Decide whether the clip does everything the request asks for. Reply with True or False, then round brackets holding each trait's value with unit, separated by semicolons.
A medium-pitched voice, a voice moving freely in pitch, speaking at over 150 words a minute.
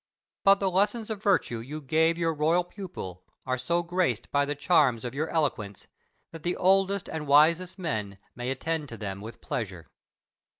True (155 Hz; 6.5 semitones; 175 wpm)